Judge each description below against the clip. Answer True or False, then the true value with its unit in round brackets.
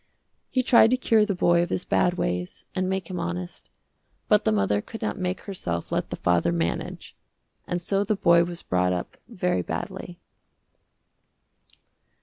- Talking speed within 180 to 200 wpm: False (165 wpm)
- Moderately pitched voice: True (175 Hz)